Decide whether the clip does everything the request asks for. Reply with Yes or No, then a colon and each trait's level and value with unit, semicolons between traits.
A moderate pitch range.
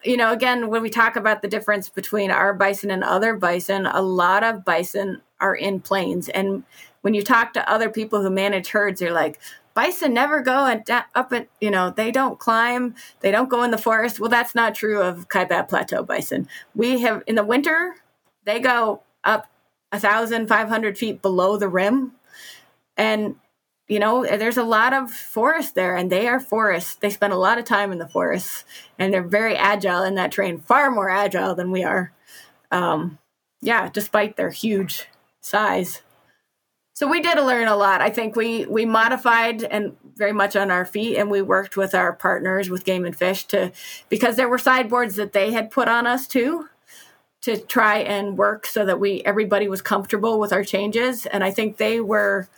Yes: average, 3.0 semitones